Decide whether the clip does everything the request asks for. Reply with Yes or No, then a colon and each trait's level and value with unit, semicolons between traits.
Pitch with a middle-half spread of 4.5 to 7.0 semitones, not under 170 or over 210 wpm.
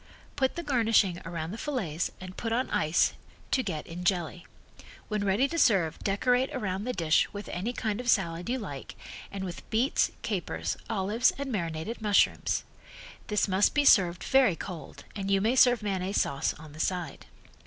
Yes: average, 5.3 semitones; average, 175 wpm